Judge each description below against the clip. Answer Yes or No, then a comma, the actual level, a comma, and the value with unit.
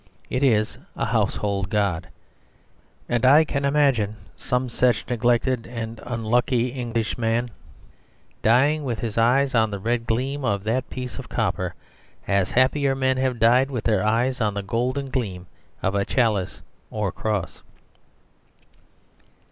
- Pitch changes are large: No, average, 3.1 semitones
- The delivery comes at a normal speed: Yes, average, 145 wpm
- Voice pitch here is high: No, low, 120 Hz